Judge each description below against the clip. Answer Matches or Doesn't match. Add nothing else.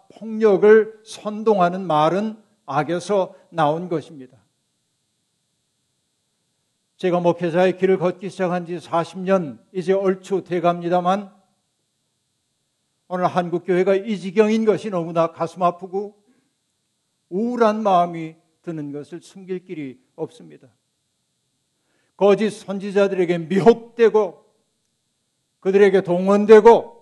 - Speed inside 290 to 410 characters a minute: Doesn't match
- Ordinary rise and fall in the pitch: Matches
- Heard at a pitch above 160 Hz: Matches